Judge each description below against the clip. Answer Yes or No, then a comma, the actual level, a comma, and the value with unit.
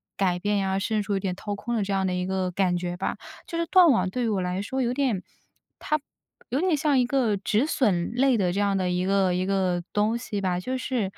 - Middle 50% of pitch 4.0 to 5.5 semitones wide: Yes, average, 5.0 semitones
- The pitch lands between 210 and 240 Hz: No, high, 200 Hz